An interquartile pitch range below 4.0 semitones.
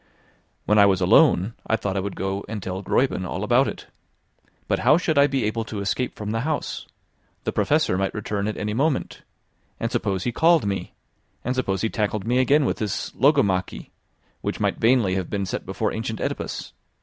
No: average, 4.8 semitones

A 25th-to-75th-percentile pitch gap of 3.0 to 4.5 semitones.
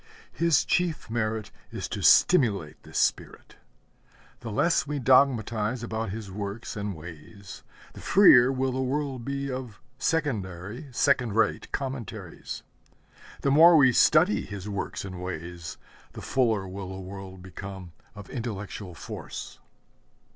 No: wide, 5.5 semitones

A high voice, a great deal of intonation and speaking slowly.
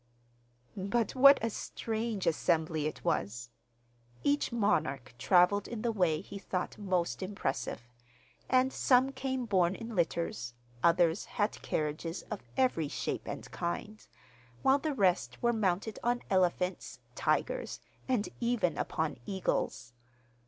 Yes: high, 195 Hz; wide, 5.7 semitones; slow, 125 wpm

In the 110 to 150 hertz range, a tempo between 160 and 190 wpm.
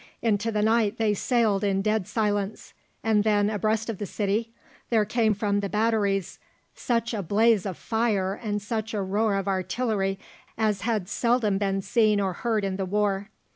No: high, 210 Hz; average, 175 wpm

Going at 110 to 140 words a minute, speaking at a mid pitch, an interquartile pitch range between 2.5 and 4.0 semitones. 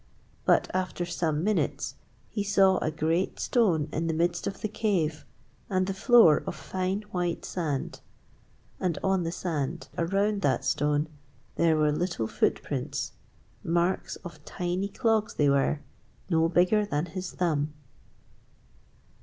Yes: slow, 135 wpm; medium, 175 Hz; average, 3.5 semitones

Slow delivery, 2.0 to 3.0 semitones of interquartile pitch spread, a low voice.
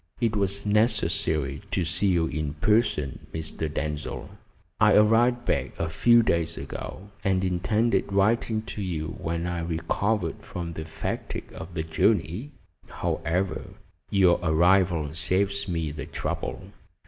No: slow, 130 wpm; average, 4.4 semitones; very low, 90 Hz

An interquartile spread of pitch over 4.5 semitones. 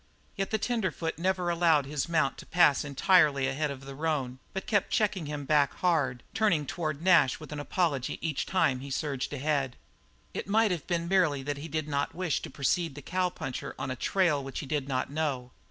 No: average, 4.2 semitones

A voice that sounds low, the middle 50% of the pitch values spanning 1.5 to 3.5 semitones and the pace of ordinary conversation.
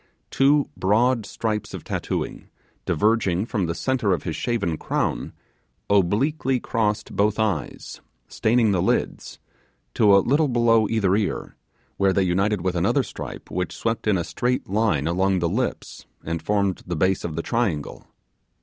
No: low, 105 Hz; average, 4.1 semitones; average, 155 wpm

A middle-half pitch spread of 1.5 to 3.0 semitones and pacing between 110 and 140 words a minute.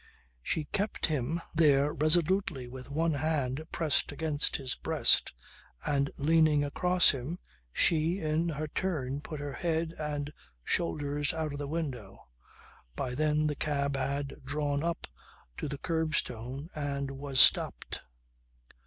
Yes: narrow, 2.4 semitones; slow, 135 wpm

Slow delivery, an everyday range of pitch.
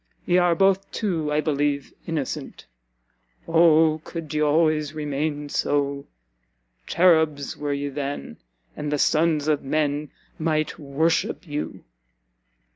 No: slow, 120 wpm; narrow, 2.0 semitones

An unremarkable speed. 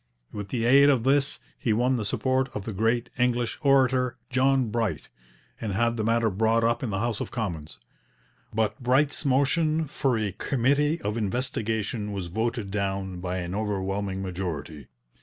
Yes: average, 165 wpm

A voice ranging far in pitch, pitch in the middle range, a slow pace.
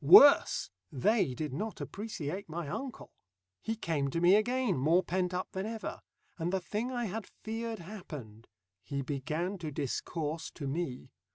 No: wide, 6.5 semitones; medium, 175 Hz; average, 160 wpm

